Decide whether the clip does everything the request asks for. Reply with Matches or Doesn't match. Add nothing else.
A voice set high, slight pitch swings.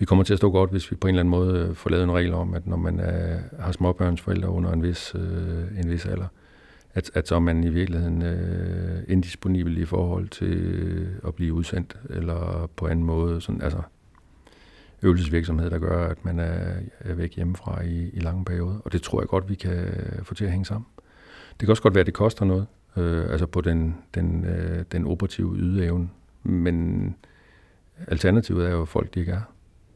Doesn't match